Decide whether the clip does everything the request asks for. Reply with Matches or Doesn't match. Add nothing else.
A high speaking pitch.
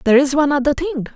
Matches